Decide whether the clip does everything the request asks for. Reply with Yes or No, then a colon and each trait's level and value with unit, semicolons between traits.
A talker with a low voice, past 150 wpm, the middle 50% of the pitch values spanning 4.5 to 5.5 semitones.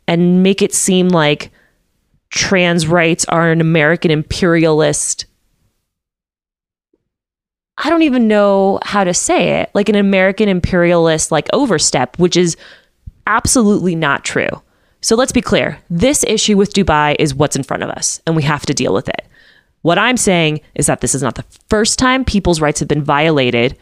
No: medium, 170 Hz; average, 170 wpm; average, 4.8 semitones